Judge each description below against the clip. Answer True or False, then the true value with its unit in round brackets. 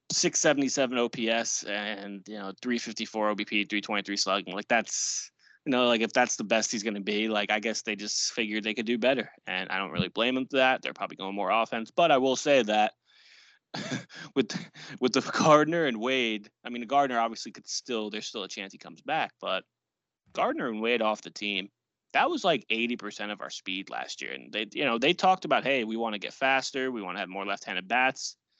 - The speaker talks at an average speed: False (220 wpm)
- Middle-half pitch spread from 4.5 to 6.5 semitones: False (3.4 semitones)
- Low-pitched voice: True (115 Hz)